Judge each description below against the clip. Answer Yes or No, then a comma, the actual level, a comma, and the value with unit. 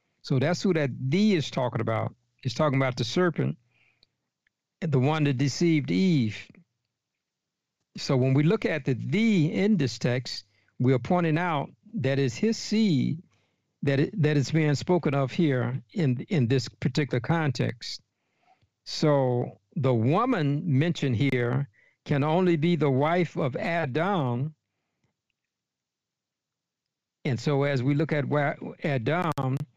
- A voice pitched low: No, medium, 145 Hz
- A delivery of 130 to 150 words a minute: Yes, average, 140 wpm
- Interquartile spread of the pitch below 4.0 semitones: No, average, 4.4 semitones